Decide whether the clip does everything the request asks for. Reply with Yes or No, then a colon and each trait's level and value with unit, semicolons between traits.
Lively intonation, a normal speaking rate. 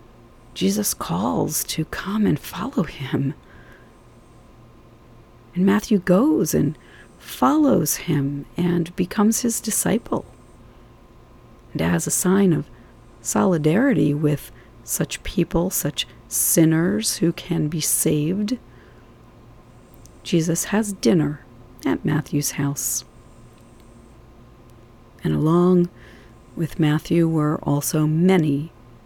No: wide, 6.8 semitones; slow, 95 wpm